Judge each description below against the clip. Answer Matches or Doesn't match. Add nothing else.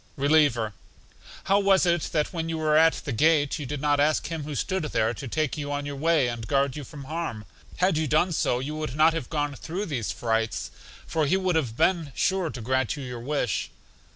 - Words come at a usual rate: Doesn't match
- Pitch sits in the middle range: Matches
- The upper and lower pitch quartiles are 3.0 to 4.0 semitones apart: Matches